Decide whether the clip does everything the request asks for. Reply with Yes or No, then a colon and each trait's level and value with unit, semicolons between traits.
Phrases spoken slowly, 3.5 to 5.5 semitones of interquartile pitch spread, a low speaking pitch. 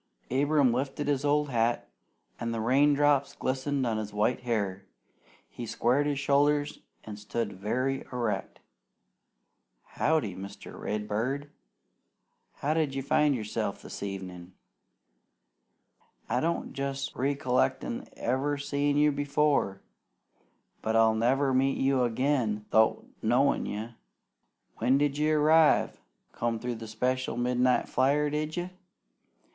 Yes: slow, 120 wpm; average, 4.1 semitones; low, 130 Hz